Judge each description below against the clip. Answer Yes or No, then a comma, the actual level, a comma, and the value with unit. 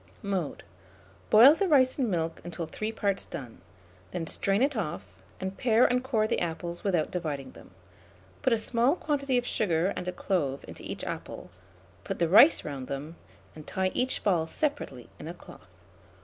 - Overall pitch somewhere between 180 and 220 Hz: Yes, high, 190 Hz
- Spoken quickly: No, average, 175 wpm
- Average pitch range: No, wide, 7.1 semitones